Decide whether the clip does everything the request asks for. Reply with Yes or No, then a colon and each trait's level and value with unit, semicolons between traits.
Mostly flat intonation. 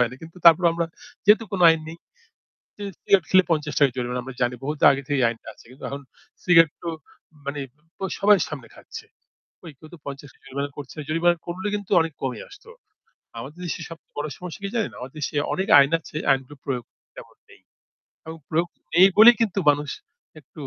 No: average, 4.1 semitones